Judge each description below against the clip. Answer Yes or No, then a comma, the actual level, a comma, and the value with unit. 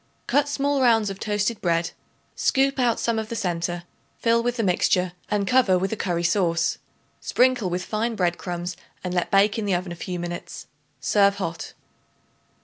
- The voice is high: Yes, high, 200 Hz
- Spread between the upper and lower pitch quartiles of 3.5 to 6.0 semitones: Yes, average, 4.7 semitones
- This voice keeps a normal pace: Yes, average, 180 wpm